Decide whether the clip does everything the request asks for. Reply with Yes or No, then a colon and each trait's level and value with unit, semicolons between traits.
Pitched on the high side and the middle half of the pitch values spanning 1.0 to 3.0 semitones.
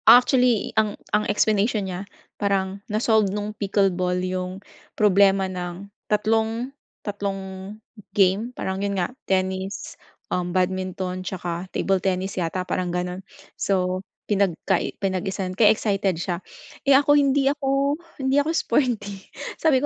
Yes: high, 195 Hz; average, 2.7 semitones